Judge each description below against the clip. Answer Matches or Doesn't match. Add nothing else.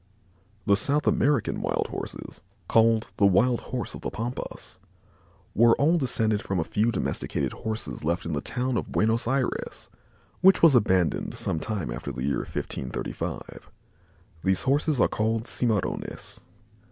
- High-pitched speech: Doesn't match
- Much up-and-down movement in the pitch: Doesn't match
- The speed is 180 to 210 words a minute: Doesn't match